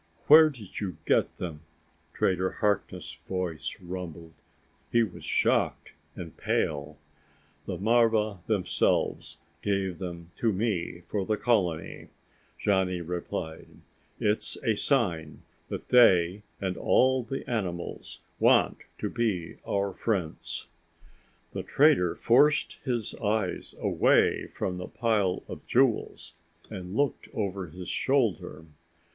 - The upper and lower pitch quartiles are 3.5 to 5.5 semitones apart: Yes, average, 4.4 semitones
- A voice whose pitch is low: Yes, very low, 95 Hz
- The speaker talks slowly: Yes, slow, 115 wpm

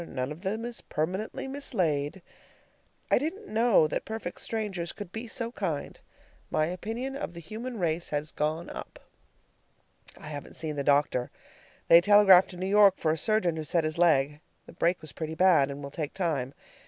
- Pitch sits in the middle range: Yes, medium, 175 Hz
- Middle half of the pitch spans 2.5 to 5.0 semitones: No, wide, 5.5 semitones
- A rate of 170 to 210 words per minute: Yes, average, 180 wpm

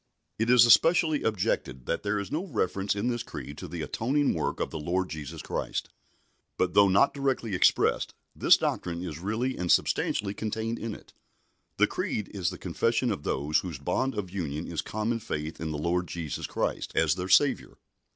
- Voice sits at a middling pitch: No, very low, 95 Hz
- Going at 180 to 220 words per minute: Yes, average, 190 wpm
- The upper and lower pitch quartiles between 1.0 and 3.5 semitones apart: No, wide, 5.6 semitones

